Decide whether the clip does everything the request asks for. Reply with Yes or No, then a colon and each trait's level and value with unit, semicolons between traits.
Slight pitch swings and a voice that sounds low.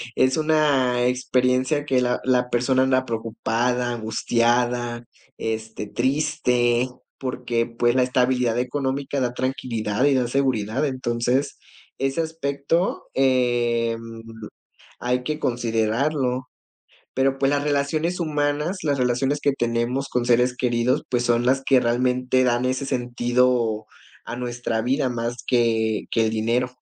Yes: narrow, 2.1 semitones; low, 125 Hz